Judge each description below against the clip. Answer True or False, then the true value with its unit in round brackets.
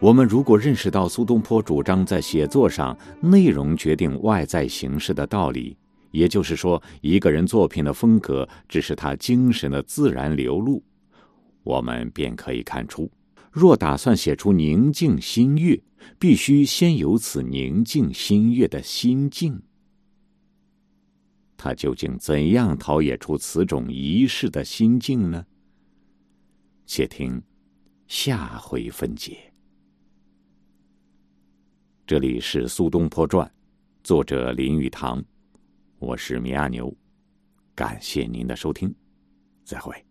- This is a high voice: False (90 Hz)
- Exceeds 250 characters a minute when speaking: False (185 characters per minute)